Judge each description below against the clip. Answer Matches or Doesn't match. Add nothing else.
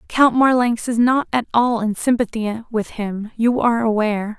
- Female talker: Matches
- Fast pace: Doesn't match